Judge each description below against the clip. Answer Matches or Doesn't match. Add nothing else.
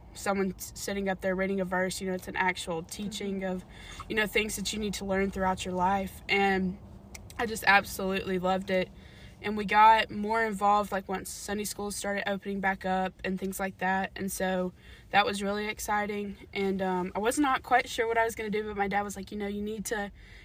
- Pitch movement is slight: Matches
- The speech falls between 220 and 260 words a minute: Matches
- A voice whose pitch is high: Matches